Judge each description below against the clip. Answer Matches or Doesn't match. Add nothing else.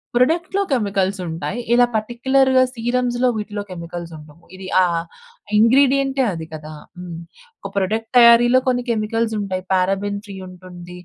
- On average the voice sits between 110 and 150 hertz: Doesn't match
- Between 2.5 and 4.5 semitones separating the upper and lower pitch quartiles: Doesn't match